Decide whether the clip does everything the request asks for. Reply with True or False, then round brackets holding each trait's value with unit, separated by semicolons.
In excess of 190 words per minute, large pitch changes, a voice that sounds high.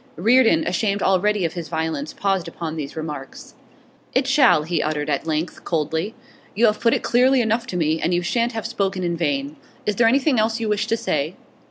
True (205 wpm; 6.2 semitones; 200 Hz)